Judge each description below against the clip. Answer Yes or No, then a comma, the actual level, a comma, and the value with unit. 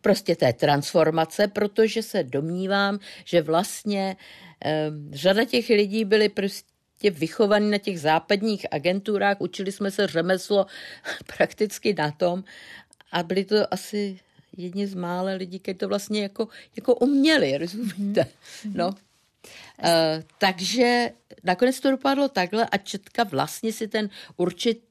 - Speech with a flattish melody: No, average, 3.4 semitones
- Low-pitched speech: No, high, 200 Hz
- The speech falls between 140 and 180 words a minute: No, average, 130 wpm